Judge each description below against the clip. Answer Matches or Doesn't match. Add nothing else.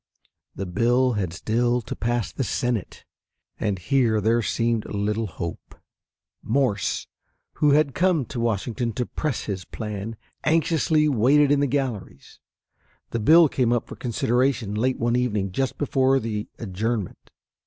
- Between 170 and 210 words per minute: Doesn't match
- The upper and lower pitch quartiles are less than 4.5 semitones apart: Matches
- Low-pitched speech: Matches